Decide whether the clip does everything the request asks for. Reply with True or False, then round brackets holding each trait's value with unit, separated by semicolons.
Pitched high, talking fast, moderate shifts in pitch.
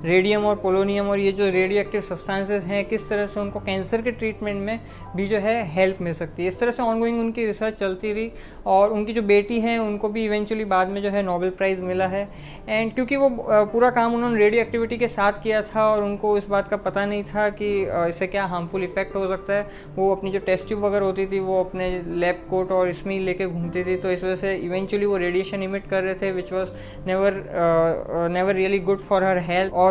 False (195 Hz; 235 wpm; 2.1 semitones)